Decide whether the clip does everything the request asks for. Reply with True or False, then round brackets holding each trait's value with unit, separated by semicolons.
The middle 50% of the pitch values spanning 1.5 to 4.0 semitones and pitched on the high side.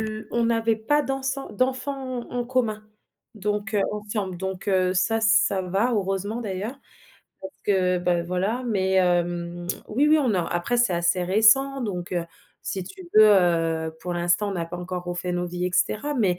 False (4.4 semitones; 195 Hz)